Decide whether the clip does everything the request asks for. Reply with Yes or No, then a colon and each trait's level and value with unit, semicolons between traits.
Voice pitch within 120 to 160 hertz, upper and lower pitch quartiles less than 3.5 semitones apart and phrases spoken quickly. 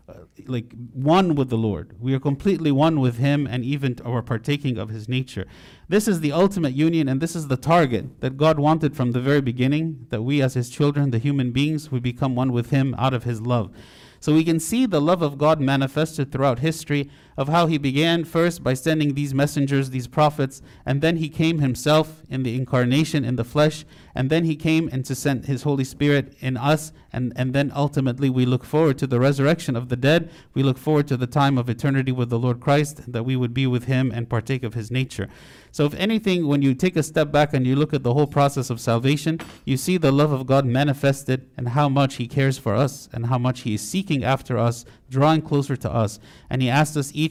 Yes: medium, 140 Hz; average, 3.1 semitones; fast, 230 wpm